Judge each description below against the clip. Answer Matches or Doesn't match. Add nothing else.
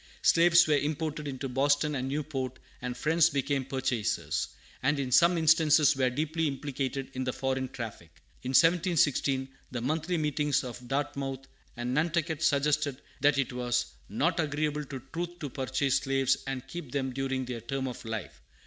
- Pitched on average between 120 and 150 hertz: Matches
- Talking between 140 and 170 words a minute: Matches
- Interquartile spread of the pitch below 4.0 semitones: Matches